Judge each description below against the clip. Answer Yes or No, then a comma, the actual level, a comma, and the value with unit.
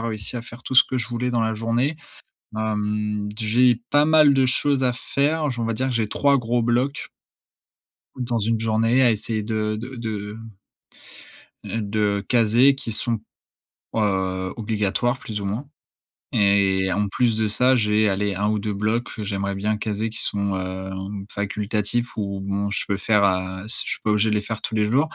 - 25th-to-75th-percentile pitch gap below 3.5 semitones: Yes, average, 2.8 semitones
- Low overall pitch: Yes, low, 110 Hz